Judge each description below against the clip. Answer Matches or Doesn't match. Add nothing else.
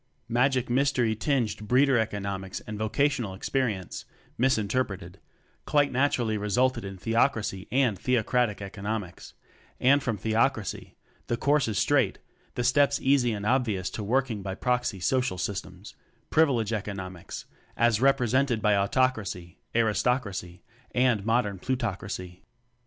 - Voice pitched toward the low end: Matches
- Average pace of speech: Doesn't match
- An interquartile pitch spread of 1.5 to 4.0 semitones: Doesn't match